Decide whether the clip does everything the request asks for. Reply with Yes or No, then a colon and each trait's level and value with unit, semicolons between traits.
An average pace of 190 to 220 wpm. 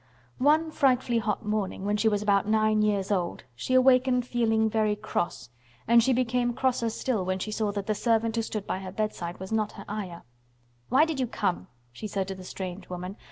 Yes: fast, 205 wpm